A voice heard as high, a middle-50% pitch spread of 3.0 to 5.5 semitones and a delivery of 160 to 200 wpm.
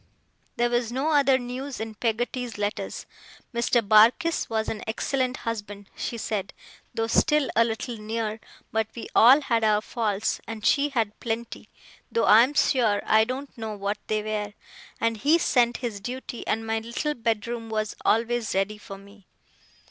No: high, 225 Hz; narrow, 2.4 semitones; average, 165 wpm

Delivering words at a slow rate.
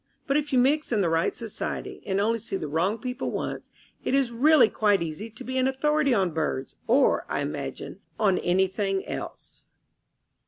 No: average, 185 wpm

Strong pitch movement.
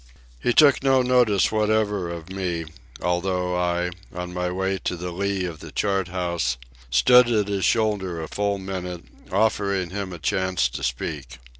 No: average, 2.7 semitones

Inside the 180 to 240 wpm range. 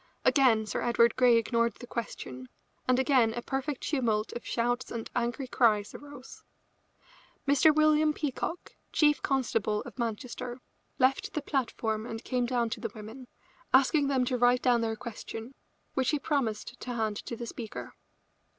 No: average, 155 wpm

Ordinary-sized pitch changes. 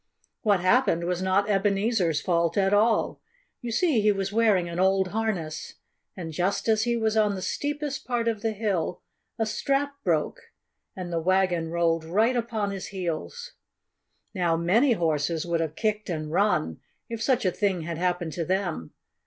Yes: average, 4.5 semitones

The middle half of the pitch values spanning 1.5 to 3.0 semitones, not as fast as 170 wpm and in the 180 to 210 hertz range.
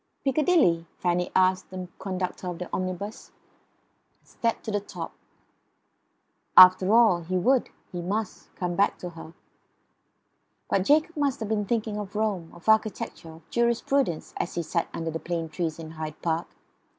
No: average, 4.1 semitones; average, 160 wpm; medium, 185 Hz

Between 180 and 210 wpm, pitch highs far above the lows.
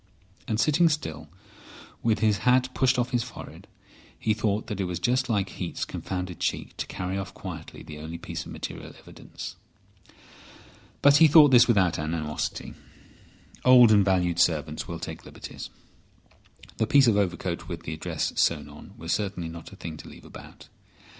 No: average, 170 wpm; wide, 6.3 semitones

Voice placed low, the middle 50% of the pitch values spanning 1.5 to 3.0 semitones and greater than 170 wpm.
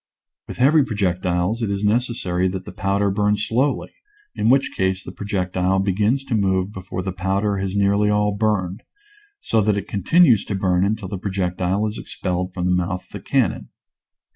Yes: low, 100 Hz; narrow, 2.4 semitones; average, 190 wpm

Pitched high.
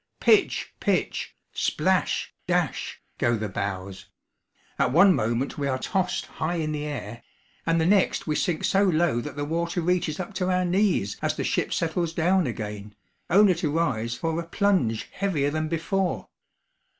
No: medium, 160 Hz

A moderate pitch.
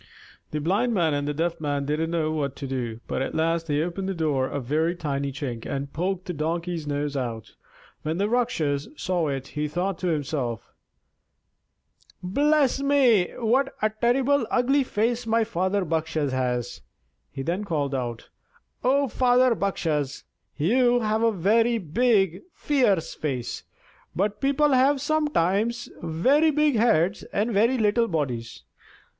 Yes: medium, 175 Hz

